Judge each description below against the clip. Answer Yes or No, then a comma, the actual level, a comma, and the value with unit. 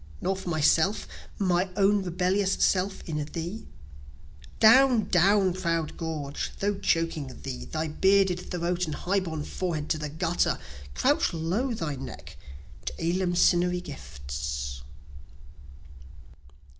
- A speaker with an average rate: No, slow, 120 wpm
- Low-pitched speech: No, medium, 175 Hz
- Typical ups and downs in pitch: Yes, average, 3.6 semitones